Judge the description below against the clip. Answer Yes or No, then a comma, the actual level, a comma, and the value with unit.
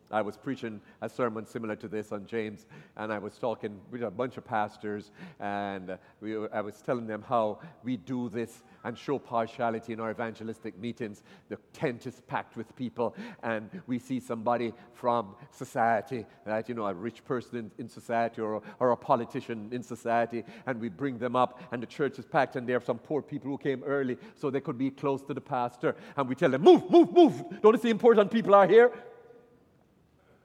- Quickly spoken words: Yes, fast, 210 wpm